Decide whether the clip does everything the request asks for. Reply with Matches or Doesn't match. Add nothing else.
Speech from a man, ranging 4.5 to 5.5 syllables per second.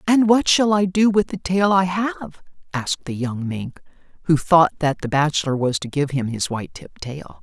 Doesn't match